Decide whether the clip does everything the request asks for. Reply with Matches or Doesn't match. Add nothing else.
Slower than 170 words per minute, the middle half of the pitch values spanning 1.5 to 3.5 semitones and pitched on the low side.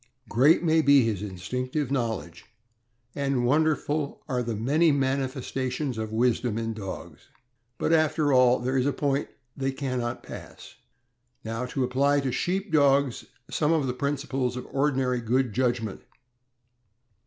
Matches